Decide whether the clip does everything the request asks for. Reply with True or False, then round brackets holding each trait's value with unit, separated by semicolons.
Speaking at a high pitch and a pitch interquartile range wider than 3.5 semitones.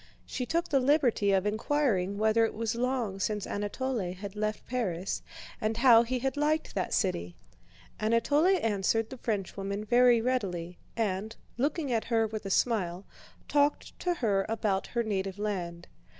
True (220 Hz; 4.2 semitones)